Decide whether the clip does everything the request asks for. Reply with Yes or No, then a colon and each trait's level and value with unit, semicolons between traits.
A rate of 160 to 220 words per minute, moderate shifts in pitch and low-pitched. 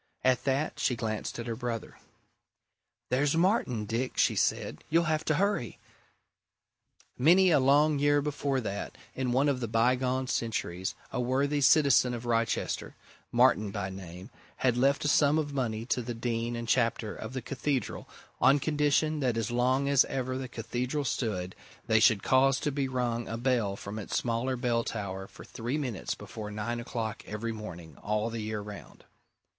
Yes: average, 170 wpm; average, 3.6 semitones; low, 125 Hz